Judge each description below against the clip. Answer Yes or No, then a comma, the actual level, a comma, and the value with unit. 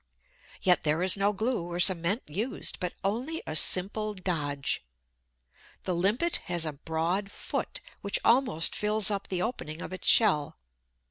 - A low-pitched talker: No, medium, 185 Hz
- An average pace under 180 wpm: Yes, average, 150 wpm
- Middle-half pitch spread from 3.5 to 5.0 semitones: Yes, average, 4.0 semitones